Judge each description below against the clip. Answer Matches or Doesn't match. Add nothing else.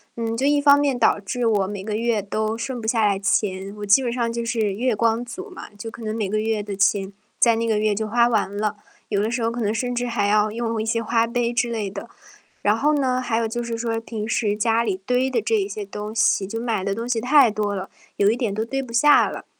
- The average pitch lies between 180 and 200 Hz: Doesn't match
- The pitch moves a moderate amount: Doesn't match